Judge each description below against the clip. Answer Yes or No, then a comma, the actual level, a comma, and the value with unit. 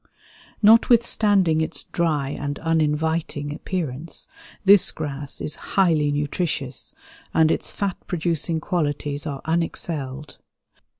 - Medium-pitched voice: Yes, medium, 160 Hz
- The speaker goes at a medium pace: No, slow, 100 wpm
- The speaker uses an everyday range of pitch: Yes, average, 3.0 semitones